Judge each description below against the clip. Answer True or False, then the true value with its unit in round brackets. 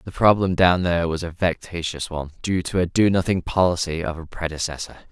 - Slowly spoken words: False (200 wpm)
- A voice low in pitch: True (85 Hz)